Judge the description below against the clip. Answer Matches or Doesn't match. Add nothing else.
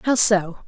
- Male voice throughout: Doesn't match